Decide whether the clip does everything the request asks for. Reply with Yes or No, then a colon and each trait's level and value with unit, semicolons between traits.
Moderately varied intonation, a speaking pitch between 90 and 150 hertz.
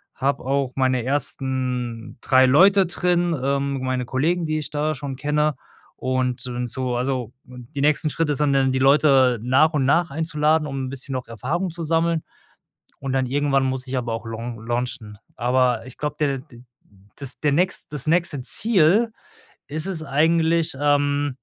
Yes: average, 3.3 semitones; medium, 140 Hz